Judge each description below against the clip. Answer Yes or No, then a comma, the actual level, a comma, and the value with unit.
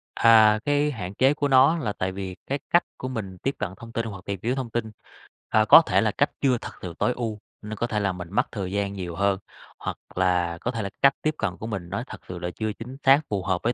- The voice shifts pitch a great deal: No, average, 4.8 semitones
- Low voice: Yes, low, 110 Hz